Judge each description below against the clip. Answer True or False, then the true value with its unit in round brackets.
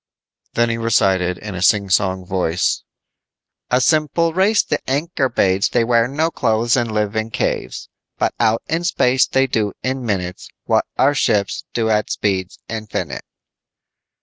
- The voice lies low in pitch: True (115 Hz)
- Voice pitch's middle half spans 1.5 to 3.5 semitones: False (5.1 semitones)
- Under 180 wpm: True (150 wpm)